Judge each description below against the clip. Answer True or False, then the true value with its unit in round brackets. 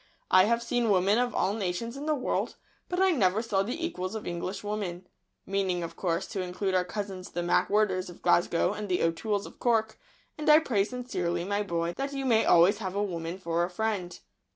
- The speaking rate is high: True (210 wpm)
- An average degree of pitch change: True (4.0 semitones)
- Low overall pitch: False (200 Hz)